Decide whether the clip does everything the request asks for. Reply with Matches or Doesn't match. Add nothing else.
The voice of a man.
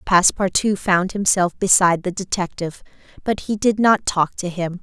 Doesn't match